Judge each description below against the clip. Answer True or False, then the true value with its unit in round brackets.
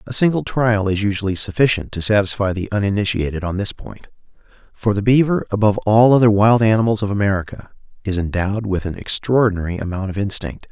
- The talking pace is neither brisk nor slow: True (175 wpm)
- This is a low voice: True (105 Hz)